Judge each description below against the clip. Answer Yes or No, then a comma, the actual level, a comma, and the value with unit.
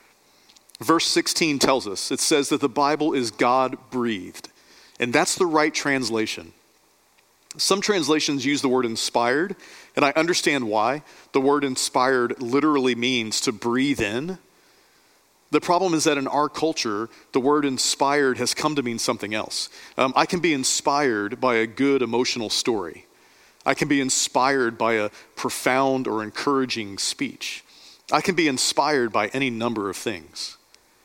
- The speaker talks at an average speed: Yes, average, 155 wpm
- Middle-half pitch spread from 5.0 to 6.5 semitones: No, average, 3.8 semitones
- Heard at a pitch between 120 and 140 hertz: Yes, low, 135 Hz